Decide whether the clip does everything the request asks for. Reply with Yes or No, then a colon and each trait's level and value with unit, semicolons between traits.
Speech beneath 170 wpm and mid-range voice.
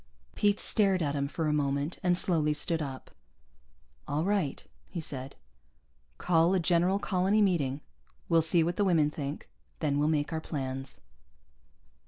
Yes: average, 155 wpm; medium, 160 Hz